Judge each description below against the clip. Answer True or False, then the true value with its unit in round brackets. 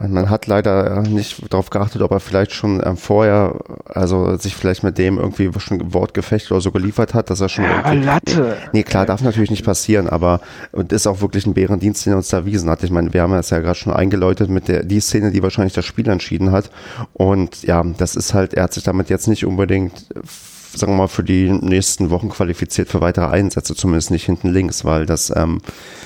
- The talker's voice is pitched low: True (95 Hz)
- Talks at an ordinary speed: False (220 wpm)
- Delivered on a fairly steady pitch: True (2.1 semitones)